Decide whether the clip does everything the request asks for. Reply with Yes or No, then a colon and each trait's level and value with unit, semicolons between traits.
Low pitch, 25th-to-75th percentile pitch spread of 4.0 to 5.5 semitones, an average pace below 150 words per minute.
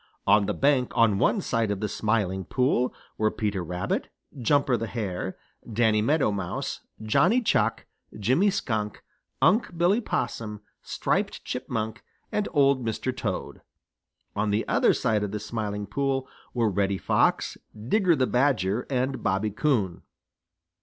Yes: low, 115 Hz; average, 4.6 semitones; average, 140 wpm